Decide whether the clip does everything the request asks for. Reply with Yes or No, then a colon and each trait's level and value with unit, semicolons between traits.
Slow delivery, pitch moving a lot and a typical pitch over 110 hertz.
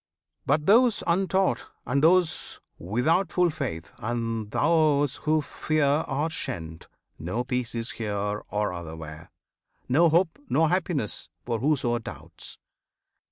Yes: slow, 125 wpm; wide, 6.8 semitones; medium, 140 Hz